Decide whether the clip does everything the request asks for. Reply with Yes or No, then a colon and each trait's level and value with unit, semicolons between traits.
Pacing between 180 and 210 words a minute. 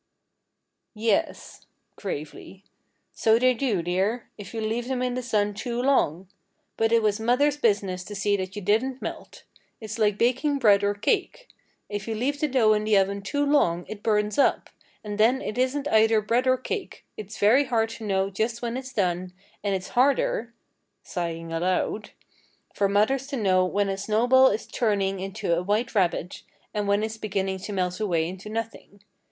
Yes: average, 185 wpm